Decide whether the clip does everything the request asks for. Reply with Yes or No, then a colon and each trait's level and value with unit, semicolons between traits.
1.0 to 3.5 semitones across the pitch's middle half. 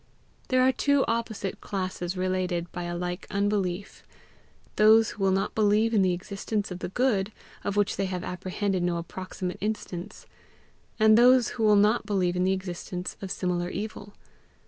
Yes: average, 2.9 semitones